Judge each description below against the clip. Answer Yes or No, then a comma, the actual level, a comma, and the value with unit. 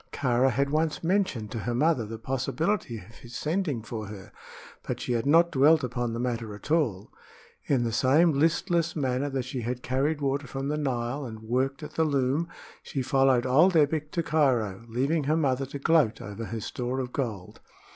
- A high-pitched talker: No, low, 135 Hz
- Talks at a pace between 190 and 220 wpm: Yes, average, 195 wpm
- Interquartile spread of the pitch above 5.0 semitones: No, average, 4.3 semitones